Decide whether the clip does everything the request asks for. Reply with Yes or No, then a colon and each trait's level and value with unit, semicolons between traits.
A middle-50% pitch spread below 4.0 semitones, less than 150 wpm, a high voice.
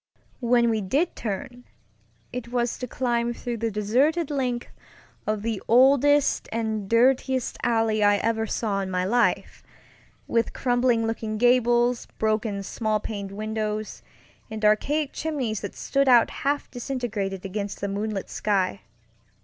Yes: average, 2.7 semitones; slow, 135 wpm; high, 230 Hz